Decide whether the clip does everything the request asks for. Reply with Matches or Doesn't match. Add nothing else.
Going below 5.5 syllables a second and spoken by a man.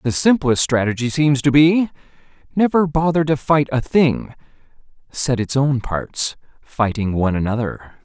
Matches